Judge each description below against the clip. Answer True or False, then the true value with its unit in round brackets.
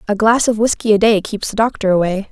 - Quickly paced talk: True (260 wpm)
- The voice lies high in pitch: True (210 Hz)